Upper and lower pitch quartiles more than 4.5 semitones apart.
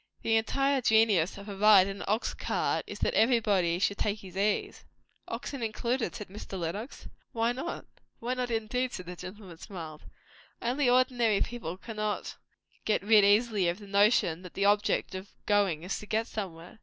No: average, 3.2 semitones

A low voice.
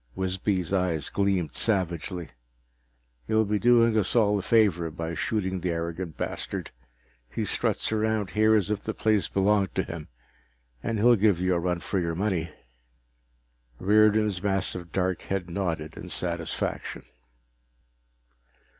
Yes: very low, 95 Hz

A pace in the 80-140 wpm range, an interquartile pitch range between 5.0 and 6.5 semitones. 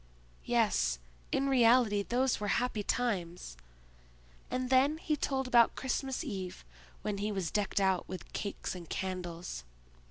Yes: slow, 135 wpm; wide, 5.5 semitones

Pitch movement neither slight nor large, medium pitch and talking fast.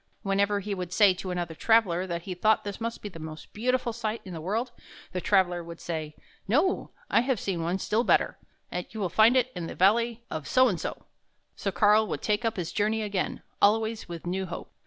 No: average, 4.0 semitones; high, 200 Hz; fast, 220 wpm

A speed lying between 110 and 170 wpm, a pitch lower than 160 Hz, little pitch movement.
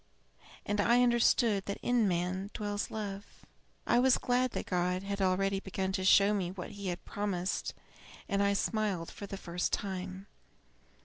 No: average, 165 wpm; high, 200 Hz; narrow, 1.9 semitones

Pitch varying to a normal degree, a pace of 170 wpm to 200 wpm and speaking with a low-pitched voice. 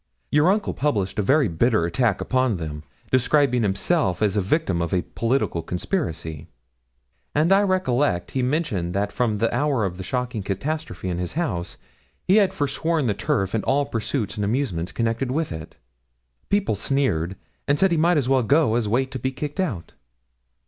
No: wide, 7.3 semitones; average, 180 wpm; low, 120 Hz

